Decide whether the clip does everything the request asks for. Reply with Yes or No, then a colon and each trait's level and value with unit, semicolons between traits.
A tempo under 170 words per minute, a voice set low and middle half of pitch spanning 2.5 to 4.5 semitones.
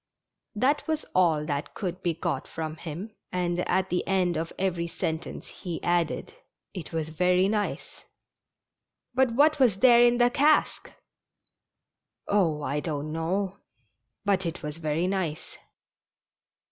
No: average, 150 wpm; medium, 180 Hz; average, 3.9 semitones